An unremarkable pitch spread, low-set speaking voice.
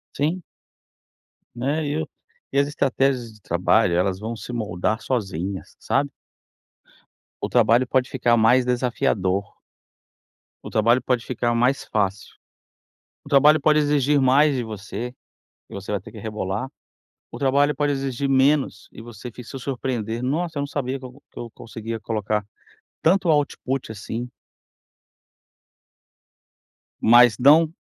Yes: average, 4.1 semitones; low, 125 Hz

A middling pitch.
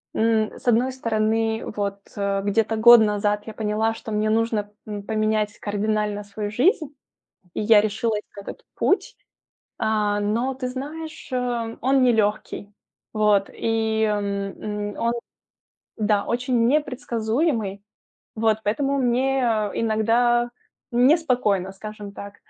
No: high, 220 Hz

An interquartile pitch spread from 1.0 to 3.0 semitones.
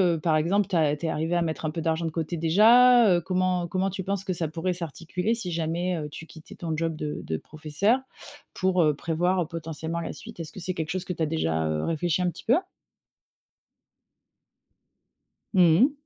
Yes: narrow, 2.6 semitones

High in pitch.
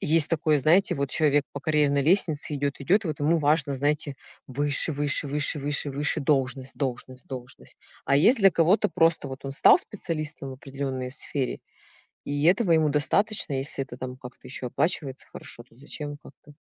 No: medium, 145 Hz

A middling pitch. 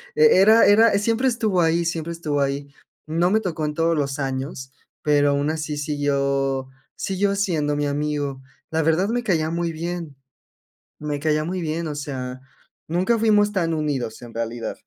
Yes: medium, 155 Hz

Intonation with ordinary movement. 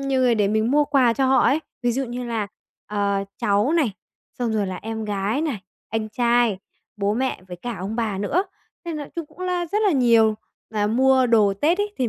Yes: average, 4.4 semitones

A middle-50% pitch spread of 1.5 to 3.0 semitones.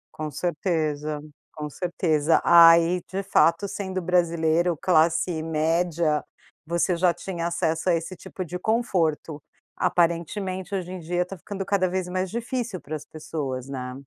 Yes: average, 2.7 semitones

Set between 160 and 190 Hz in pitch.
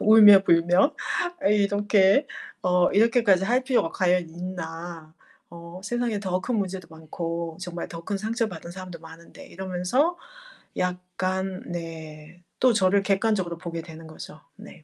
Yes: medium, 185 Hz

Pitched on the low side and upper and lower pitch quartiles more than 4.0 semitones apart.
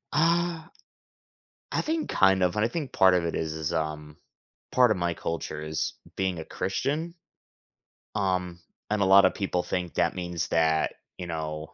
Yes: very low, 90 Hz; average, 4.8 semitones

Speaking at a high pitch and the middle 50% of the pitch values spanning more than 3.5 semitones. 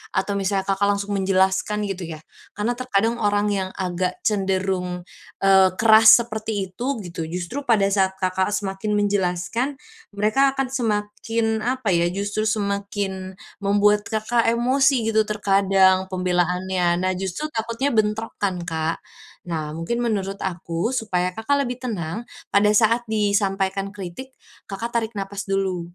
No: high, 200 Hz; average, 2.7 semitones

